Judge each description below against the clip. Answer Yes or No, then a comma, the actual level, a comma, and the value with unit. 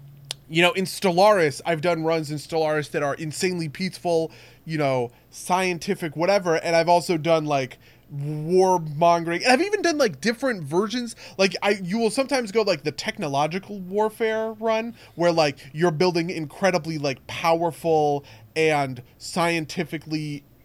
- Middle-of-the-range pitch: Yes, medium, 170 Hz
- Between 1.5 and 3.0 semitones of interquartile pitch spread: No, average, 3.9 semitones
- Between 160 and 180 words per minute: No, average, 150 wpm